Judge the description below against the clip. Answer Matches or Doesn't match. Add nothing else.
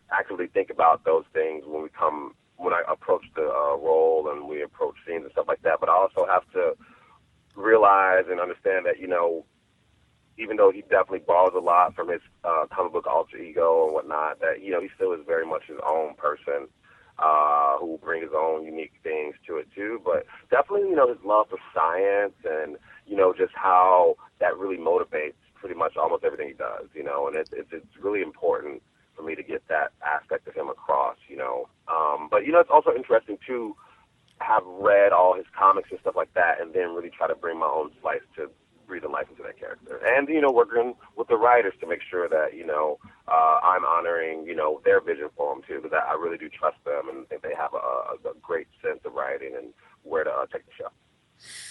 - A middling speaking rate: Doesn't match